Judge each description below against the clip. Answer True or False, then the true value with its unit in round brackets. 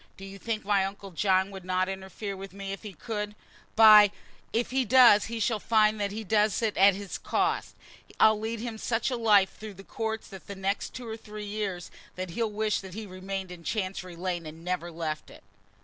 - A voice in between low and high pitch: False (200 Hz)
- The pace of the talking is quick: True (225 wpm)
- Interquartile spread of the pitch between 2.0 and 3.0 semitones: True (2.4 semitones)